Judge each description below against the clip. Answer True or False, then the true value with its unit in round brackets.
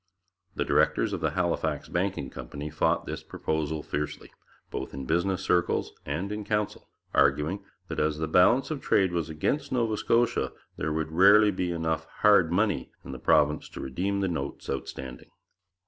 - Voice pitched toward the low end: True (85 Hz)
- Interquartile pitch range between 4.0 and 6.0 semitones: True (4.9 semitones)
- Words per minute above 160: True (170 wpm)